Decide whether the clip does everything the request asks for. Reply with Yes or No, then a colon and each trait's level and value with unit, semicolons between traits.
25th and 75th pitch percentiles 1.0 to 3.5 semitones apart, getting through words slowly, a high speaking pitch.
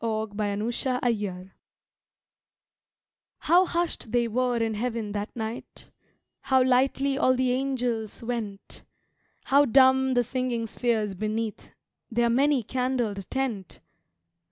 Yes: average, 3.1 semitones; slow, 110 wpm; high, 240 Hz